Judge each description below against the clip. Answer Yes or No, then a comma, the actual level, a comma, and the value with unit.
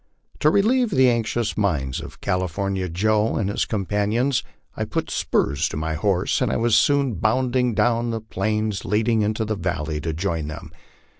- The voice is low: Yes, low, 105 Hz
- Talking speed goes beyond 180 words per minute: No, average, 175 wpm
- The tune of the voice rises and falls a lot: No, average, 4.4 semitones